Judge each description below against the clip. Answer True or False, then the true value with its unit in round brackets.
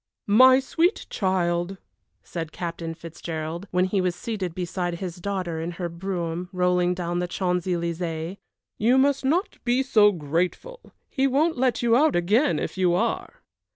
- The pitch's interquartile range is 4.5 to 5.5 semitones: True (5.1 semitones)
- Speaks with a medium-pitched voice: True (180 Hz)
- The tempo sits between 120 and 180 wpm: True (155 wpm)